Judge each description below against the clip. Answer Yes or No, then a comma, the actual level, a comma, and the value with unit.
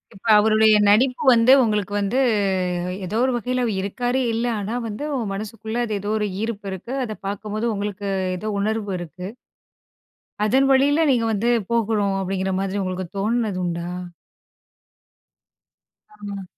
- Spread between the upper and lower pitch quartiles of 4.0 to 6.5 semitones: No, average, 2.7 semitones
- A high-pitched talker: Yes, high, 210 Hz